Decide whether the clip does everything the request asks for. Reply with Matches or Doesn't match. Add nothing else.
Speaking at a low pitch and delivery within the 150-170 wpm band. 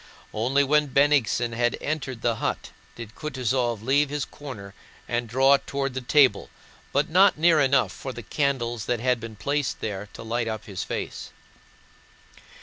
Matches